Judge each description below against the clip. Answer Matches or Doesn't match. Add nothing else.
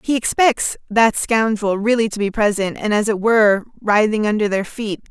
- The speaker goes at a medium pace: Matches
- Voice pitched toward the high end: Matches